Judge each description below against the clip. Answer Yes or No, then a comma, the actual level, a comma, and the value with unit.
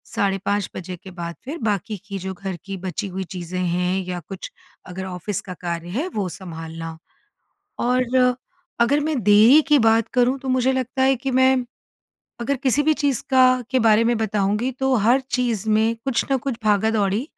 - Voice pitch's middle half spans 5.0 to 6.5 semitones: Yes, wide, 5.4 semitones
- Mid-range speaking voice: No, high, 215 Hz